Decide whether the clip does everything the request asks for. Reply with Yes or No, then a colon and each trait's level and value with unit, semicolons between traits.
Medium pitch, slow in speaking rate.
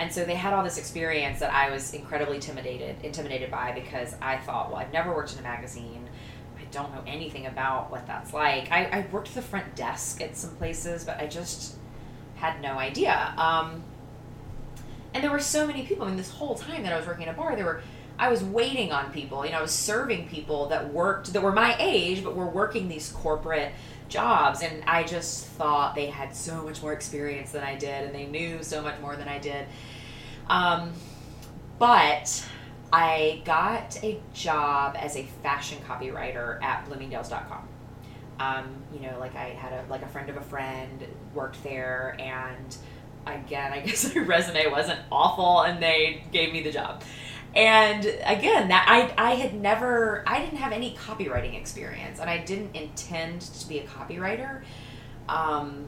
No: medium, 145 Hz; average, 190 wpm